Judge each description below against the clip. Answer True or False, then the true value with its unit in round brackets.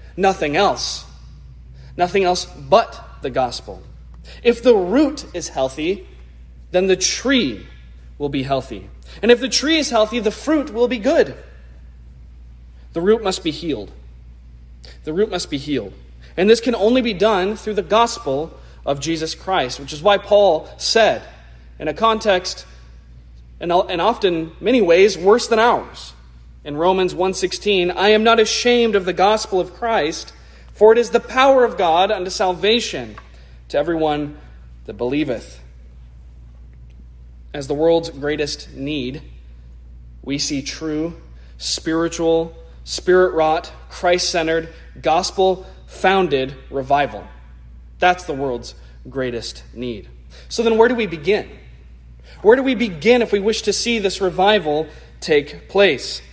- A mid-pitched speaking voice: True (160 Hz)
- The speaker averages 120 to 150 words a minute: True (135 wpm)